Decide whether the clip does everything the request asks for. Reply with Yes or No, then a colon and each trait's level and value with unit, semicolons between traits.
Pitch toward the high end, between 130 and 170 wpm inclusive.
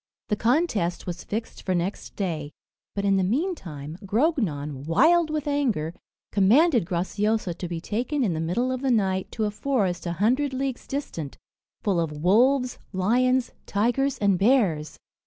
Yes: high, 210 Hz; average, 155 wpm